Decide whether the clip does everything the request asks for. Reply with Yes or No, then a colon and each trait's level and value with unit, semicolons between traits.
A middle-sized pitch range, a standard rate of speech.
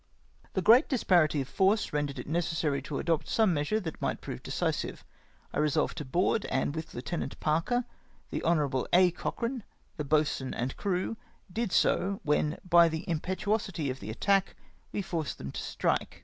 Yes: average, 4.6 semitones; average, 175 wpm